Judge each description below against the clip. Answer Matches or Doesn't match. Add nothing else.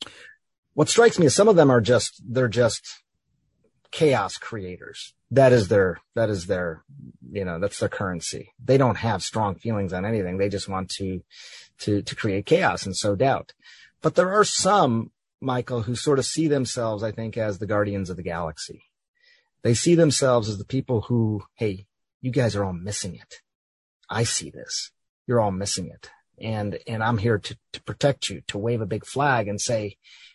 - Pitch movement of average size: Matches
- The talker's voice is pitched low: Matches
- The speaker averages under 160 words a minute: Doesn't match